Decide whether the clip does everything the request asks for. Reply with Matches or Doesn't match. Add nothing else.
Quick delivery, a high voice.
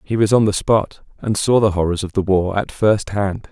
Doesn't match